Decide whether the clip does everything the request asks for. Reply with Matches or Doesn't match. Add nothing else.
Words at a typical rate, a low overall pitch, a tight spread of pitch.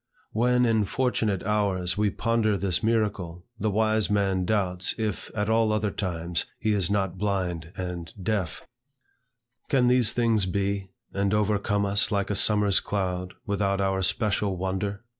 Matches